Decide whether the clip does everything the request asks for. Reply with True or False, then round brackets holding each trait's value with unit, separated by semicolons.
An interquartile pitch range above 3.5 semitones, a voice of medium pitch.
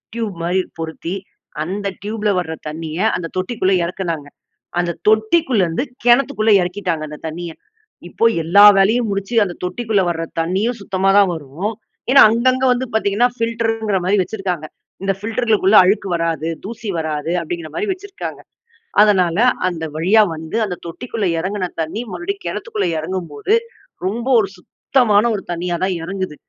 False (4.7 semitones; 195 Hz)